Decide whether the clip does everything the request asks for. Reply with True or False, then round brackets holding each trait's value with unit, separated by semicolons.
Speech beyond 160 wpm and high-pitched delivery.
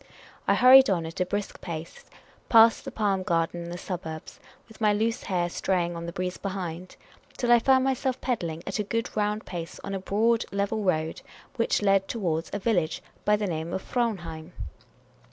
True (185 wpm; 195 Hz)